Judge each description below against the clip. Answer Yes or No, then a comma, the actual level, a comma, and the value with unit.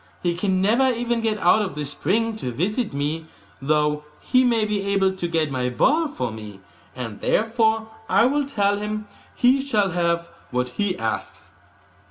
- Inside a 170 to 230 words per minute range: Yes, average, 175 wpm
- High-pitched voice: Yes, high, 195 Hz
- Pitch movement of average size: No, wide, 7.0 semitones